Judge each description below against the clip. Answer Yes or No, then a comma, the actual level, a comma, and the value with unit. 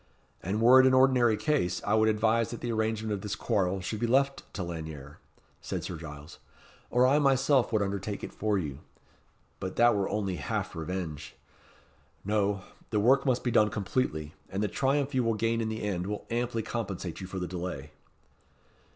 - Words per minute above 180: Yes, average, 190 wpm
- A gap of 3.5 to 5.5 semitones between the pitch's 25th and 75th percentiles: Yes, average, 4.5 semitones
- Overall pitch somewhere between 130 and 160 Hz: No, low, 105 Hz